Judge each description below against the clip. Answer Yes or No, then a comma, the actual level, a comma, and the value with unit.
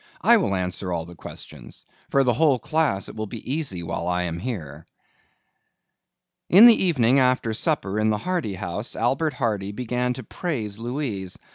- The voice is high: No, low, 115 Hz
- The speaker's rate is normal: Yes, average, 165 wpm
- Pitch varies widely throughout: Yes, wide, 6.1 semitones